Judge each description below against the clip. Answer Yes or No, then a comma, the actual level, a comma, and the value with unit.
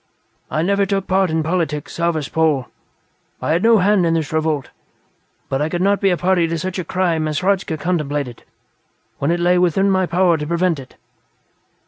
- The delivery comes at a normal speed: Yes, average, 185 wpm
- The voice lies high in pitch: No, medium, 170 Hz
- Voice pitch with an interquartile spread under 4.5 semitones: Yes, average, 3.0 semitones